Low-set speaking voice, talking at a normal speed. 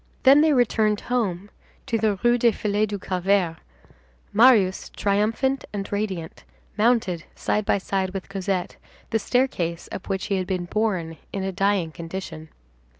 No: high, 200 Hz; average, 150 wpm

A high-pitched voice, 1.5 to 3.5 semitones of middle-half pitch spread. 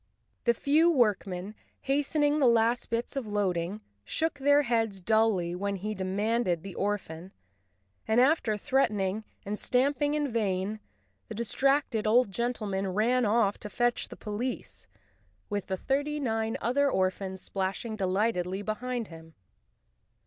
No: high, 220 Hz; average, 4.4 semitones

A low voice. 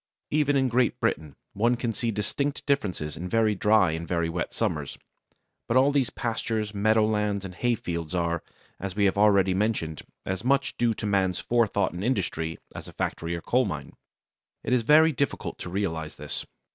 Yes: low, 105 Hz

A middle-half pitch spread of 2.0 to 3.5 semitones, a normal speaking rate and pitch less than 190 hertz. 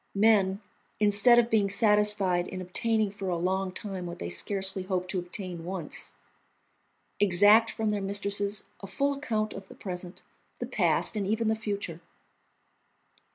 No: narrow, 2.5 semitones; average, 155 wpm; high, 200 Hz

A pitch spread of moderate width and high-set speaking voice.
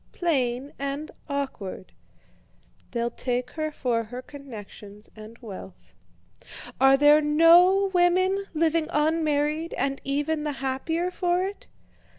Yes: average, 4.6 semitones; very high, 290 Hz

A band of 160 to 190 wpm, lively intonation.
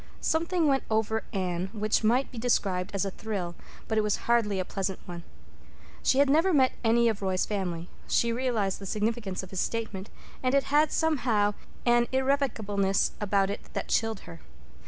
No: average, 180 wpm; average, 4.3 semitones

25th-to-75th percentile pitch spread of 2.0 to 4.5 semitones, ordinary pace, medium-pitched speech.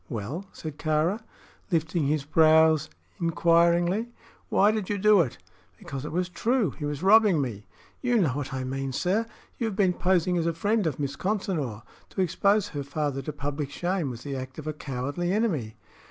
No: average, 5.1 semitones; average, 185 wpm; medium, 160 Hz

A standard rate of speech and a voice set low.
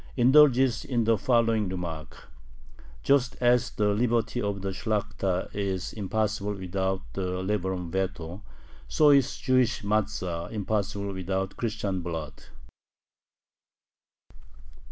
No: slow, 110 wpm; low, 100 Hz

